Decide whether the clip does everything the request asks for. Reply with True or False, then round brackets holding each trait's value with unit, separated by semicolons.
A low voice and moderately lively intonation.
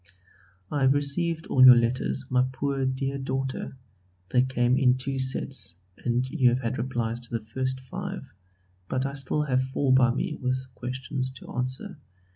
False (130 Hz; 1.4 semitones)